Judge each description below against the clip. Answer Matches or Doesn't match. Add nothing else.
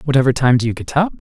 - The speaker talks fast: Matches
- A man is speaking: Matches